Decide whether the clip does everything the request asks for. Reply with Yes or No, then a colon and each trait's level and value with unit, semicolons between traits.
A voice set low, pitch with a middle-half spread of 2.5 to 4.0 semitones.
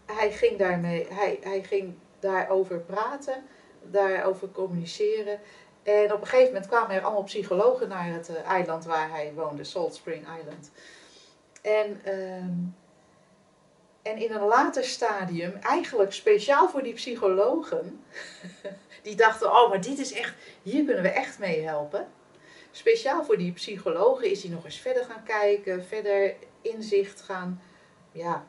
No: high, 200 Hz; average, 3.7 semitones